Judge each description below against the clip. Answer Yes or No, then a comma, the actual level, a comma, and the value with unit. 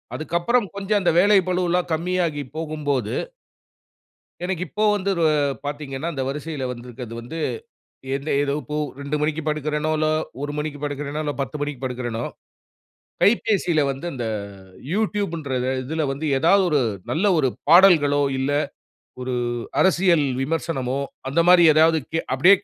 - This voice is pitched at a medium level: Yes, medium, 155 Hz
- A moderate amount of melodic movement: Yes, average, 3.9 semitones